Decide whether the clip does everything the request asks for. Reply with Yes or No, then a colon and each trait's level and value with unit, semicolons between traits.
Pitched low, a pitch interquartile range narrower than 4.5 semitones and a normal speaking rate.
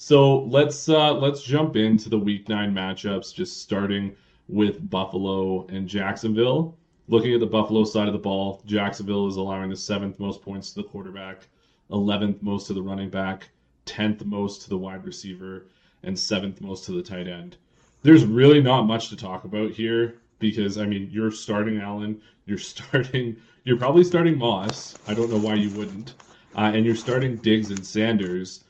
Yes: low, 105 Hz; average, 2.9 semitones; average, 180 wpm